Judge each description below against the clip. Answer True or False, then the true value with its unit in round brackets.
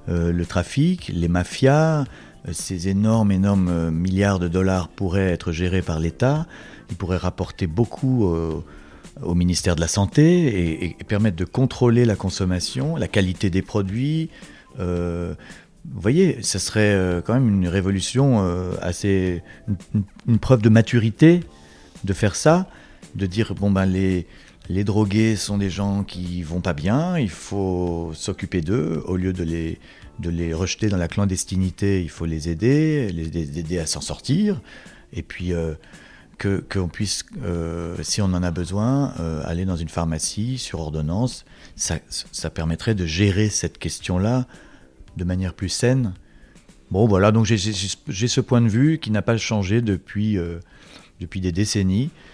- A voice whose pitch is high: False (95 Hz)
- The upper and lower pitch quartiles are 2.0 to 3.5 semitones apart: False (4.3 semitones)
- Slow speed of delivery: False (165 wpm)